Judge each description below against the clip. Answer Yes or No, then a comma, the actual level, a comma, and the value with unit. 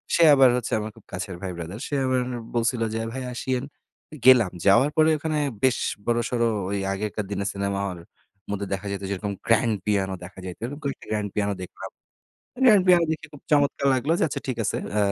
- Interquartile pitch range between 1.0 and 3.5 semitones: No, average, 4.9 semitones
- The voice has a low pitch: Yes, low, 115 Hz